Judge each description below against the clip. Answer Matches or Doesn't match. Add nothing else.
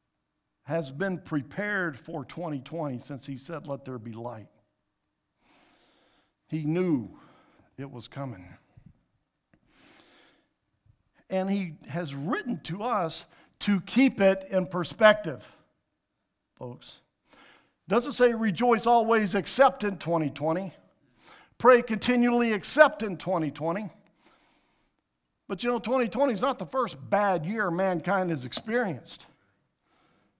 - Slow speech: Matches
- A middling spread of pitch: Doesn't match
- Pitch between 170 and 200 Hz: Matches